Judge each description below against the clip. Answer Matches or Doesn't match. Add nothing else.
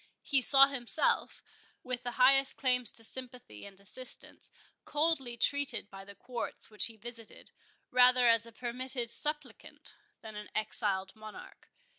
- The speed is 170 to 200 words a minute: Doesn't match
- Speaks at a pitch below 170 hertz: Doesn't match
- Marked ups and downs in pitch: Doesn't match